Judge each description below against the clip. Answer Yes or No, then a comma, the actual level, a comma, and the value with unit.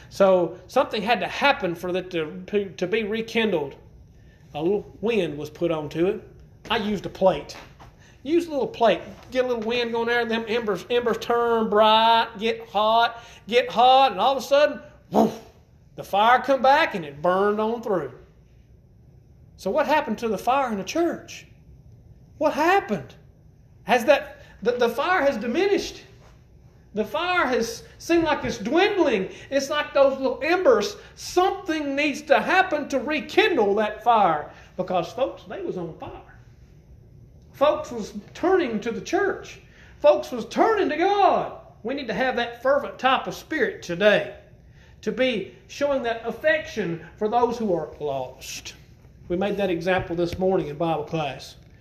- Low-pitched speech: No, high, 235 Hz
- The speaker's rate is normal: Yes, average, 165 wpm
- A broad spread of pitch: Yes, wide, 6.5 semitones